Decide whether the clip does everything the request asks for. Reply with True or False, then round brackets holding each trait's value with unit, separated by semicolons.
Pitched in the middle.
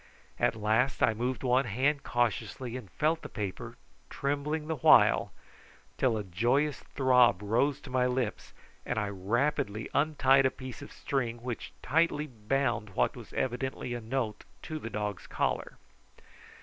False (125 Hz)